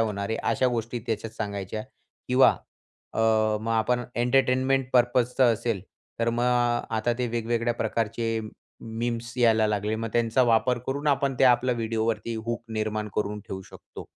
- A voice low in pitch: Yes, low, 115 Hz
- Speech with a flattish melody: Yes, narrow, 1.7 semitones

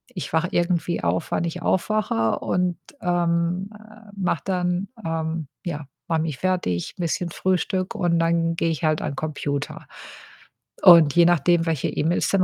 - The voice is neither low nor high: Yes, medium, 170 Hz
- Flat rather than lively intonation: Yes, narrow, 2.1 semitones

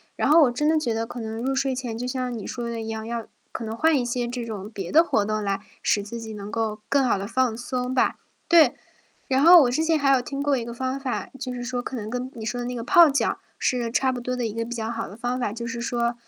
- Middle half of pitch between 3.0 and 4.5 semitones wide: No, narrow, 2.4 semitones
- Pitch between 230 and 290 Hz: Yes, high, 245 Hz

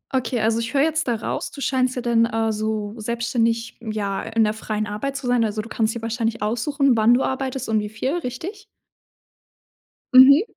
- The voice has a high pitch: Yes, high, 230 Hz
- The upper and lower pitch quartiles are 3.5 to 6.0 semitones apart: No, average, 2.9 semitones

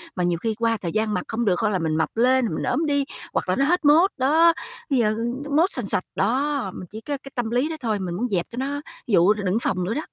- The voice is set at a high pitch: Yes, high, 230 Hz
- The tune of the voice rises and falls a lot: Yes, wide, 6.2 semitones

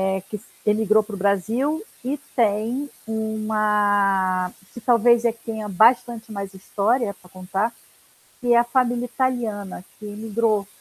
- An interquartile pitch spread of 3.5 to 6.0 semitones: No, average, 2.9 semitones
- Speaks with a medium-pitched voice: No, high, 220 Hz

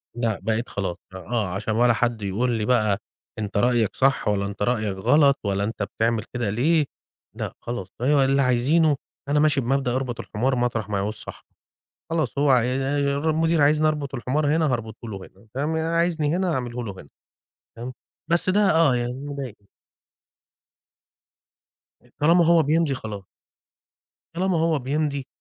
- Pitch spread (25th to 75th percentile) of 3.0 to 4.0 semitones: No, average, 5.2 semitones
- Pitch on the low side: Yes, low, 125 Hz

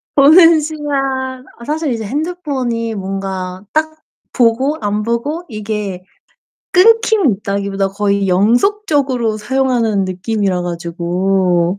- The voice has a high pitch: Yes, high, 230 Hz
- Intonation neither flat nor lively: No, wide, 6.8 semitones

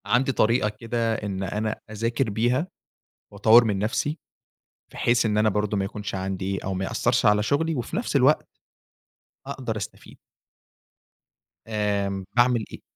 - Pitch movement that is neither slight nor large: Yes, average, 3.0 semitones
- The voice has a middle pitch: No, low, 110 Hz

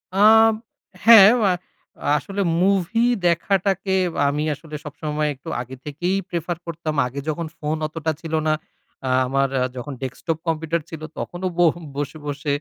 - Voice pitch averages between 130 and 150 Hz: No, medium, 160 Hz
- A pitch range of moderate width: Yes, average, 4.1 semitones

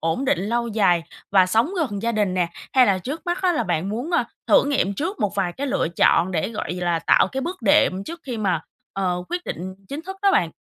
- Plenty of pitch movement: Yes, wide, 7.5 semitones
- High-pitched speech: Yes, high, 210 Hz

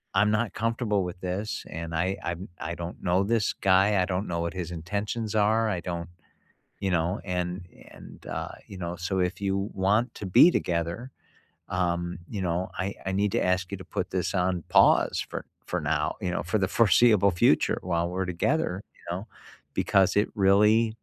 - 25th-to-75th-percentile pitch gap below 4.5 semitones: Yes, average, 2.8 semitones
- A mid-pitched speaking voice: No, very low, 95 Hz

